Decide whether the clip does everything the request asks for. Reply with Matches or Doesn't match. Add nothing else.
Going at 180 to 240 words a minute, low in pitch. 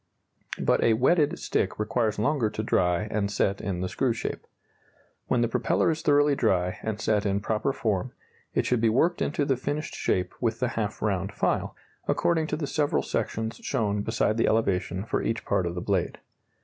Matches